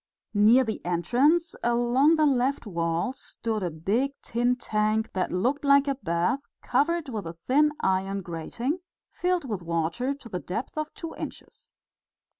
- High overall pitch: Yes, high, 240 Hz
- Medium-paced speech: Yes, average, 155 wpm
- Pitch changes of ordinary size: No, wide, 6.9 semitones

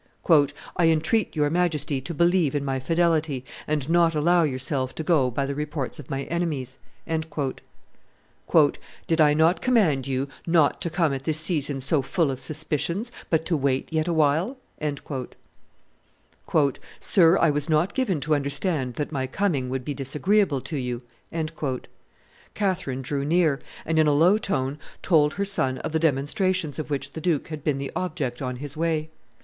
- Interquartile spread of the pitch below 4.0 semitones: Yes, average, 3.4 semitones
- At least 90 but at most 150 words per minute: No, average, 165 wpm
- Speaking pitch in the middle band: Yes, medium, 150 Hz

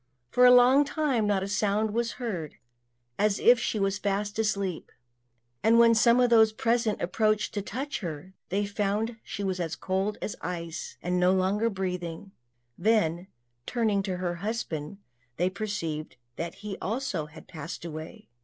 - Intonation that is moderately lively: Yes, average, 3.7 semitones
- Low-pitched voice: No, high, 200 Hz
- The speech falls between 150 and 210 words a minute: Yes, average, 165 wpm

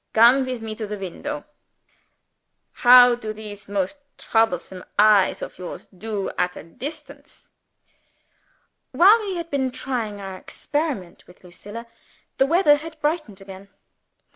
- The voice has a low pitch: No, high, 225 Hz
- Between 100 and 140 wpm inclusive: Yes, slow, 135 wpm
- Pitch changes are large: Yes, wide, 6.6 semitones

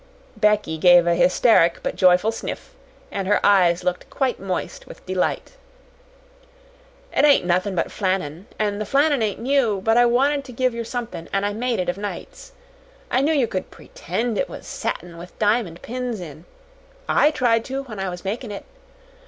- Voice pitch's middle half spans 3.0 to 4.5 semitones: No, average, 5.1 semitones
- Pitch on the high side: Yes, high, 210 Hz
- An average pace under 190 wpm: Yes, average, 180 wpm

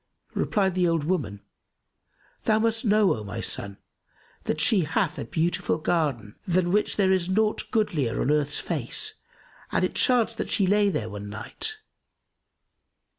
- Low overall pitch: No, medium, 175 Hz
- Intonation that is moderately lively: No, wide, 6.5 semitones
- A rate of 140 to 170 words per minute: Yes, average, 155 wpm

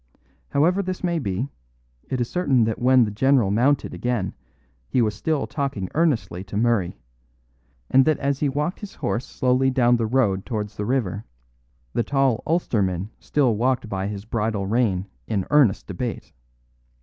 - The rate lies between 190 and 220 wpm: No, average, 160 wpm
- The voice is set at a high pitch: No, low, 120 Hz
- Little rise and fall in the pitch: No, average, 4.9 semitones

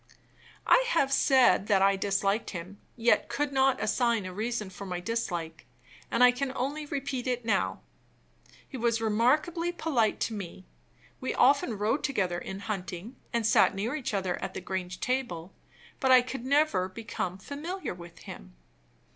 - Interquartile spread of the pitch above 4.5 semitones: Yes, wide, 5.6 semitones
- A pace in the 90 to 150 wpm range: No, average, 165 wpm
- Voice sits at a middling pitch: No, high, 230 Hz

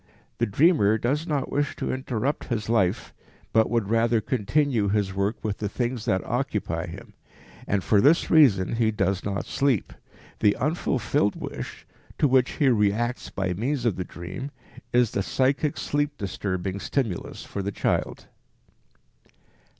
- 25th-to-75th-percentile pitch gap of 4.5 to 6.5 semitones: Yes, average, 4.9 semitones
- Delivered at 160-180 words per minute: No, average, 150 wpm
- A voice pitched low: Yes, low, 115 Hz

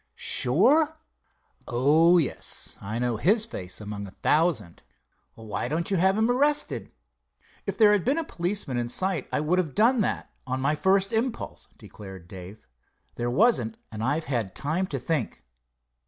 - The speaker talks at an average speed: Yes, average, 160 wpm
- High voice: No, medium, 155 Hz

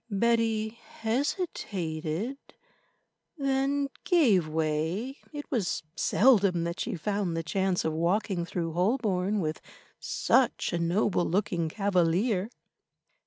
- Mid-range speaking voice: No, high, 195 Hz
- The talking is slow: Yes, slow, 105 wpm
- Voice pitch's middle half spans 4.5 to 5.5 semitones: Yes, average, 5.2 semitones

